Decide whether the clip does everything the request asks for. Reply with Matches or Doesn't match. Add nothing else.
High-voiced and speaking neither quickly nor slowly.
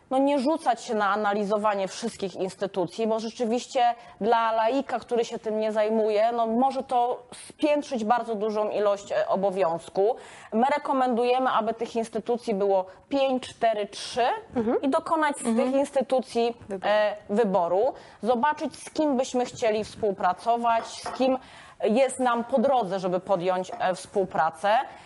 Matches